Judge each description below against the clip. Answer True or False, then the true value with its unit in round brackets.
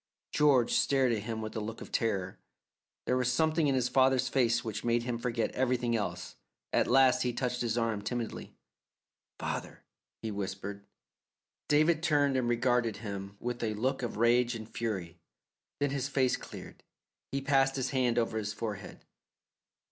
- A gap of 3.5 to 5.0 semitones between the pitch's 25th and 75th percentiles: False (3.0 semitones)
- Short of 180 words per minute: True (165 wpm)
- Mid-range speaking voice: False (120 Hz)